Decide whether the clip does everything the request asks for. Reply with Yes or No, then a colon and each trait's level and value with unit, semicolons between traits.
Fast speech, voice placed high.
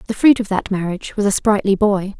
Yes: fast, 245 wpm; high, 205 Hz